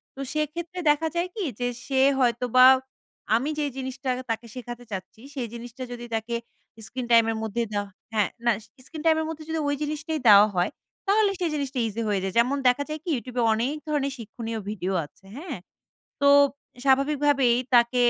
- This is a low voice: No, very high, 255 Hz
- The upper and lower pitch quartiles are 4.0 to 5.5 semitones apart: Yes, average, 4.3 semitones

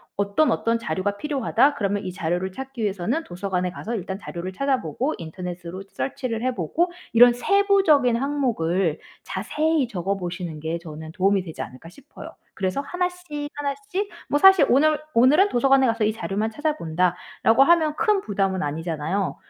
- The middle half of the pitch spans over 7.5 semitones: Yes, wide, 8.0 semitones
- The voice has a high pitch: Yes, high, 220 Hz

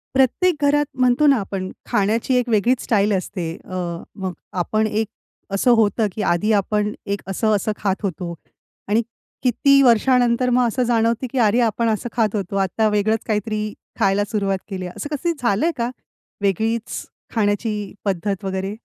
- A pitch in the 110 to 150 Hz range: No, high, 215 Hz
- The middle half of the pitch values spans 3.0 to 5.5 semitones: Yes, average, 3.3 semitones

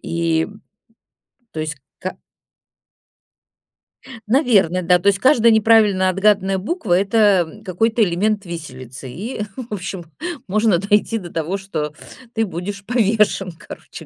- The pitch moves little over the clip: No, average, 3.8 semitones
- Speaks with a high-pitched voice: Yes, high, 195 Hz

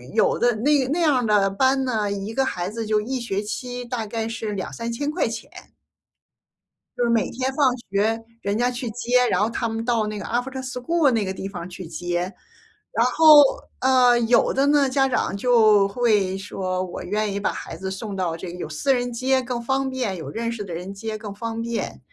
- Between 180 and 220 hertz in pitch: No, high, 230 Hz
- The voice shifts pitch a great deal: No, average, 3.9 semitones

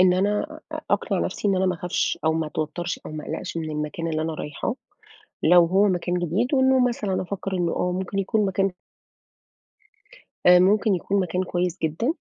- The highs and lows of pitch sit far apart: No, average, 3.0 semitones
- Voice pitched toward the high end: No, medium, 180 Hz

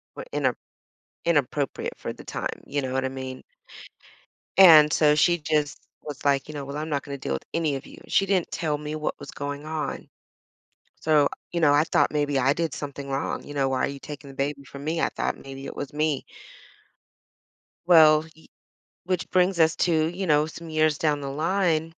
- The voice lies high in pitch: No, medium, 150 Hz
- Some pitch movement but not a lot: No, narrow, 2.3 semitones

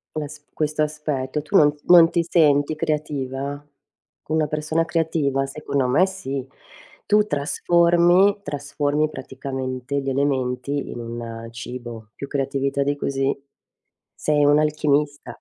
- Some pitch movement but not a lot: No, narrow, 2.2 semitones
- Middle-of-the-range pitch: Yes, medium, 145 Hz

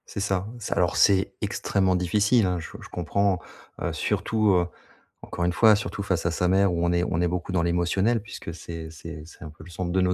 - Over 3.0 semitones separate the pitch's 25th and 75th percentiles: No, narrow, 2.5 semitones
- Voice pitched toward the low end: Yes, very low, 90 Hz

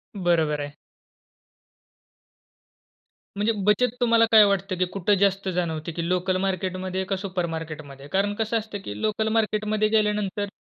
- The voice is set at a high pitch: Yes, high, 195 Hz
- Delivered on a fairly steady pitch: No, average, 3.2 semitones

